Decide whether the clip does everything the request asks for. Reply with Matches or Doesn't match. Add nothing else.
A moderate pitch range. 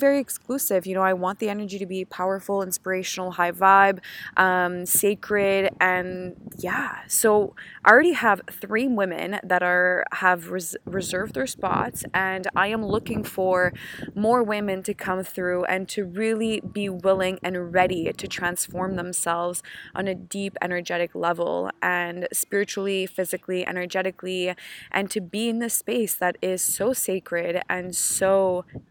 Doesn't match